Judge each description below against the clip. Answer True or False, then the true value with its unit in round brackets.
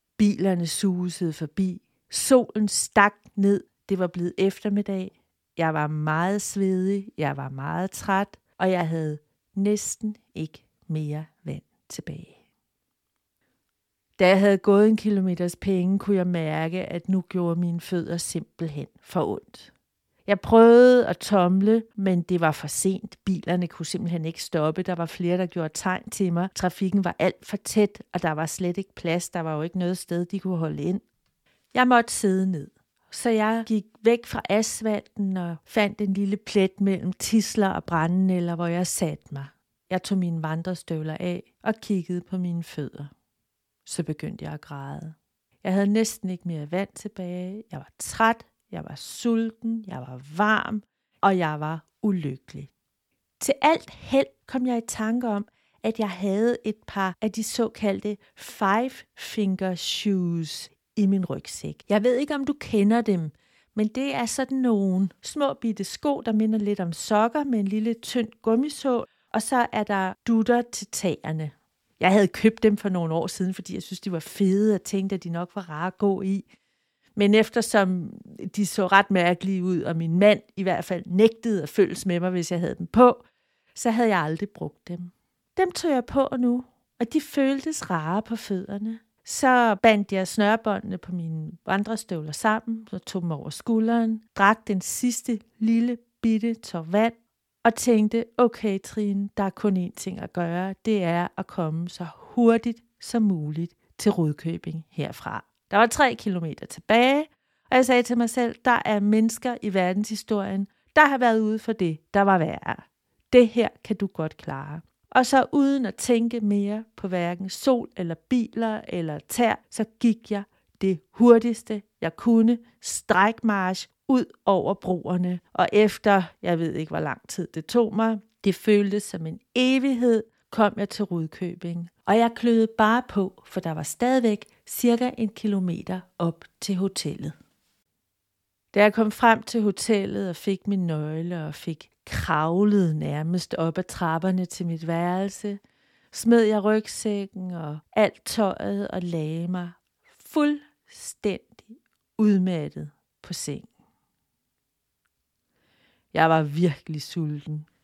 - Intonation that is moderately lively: True (4.2 semitones)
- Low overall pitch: False (195 Hz)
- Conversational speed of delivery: True (165 wpm)